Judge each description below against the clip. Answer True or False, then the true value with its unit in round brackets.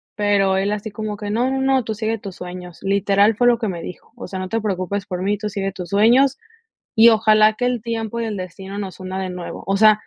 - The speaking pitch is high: True (205 Hz)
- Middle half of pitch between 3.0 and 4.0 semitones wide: False (2.6 semitones)